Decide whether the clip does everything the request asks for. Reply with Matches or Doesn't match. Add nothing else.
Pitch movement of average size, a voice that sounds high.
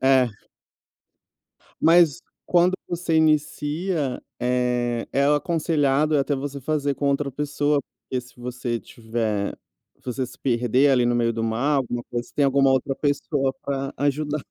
Doesn't match